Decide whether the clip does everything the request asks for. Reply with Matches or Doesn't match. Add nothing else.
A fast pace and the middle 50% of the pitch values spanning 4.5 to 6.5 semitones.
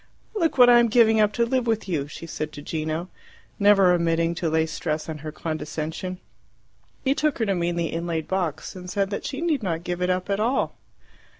Matches